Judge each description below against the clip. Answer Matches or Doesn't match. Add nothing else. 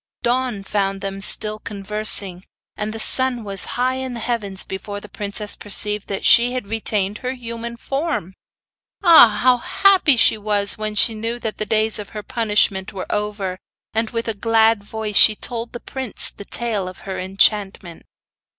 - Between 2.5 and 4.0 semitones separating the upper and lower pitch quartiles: Matches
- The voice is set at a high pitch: Matches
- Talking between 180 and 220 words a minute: Doesn't match